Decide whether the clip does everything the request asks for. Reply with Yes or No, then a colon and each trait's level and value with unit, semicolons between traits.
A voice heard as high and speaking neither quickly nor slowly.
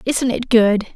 Yes: high, 230 Hz; average, 190 wpm